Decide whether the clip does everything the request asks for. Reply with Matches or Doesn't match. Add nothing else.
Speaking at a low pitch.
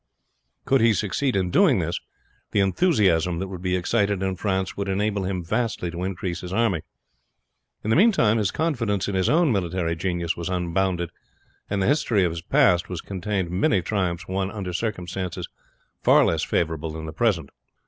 Matches